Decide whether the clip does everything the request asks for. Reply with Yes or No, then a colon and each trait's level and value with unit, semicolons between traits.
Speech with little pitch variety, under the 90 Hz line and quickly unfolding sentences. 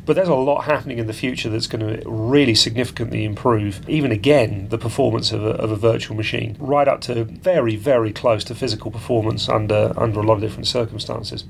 No: narrow, 2.3 semitones; low, 115 Hz; fast, 210 wpm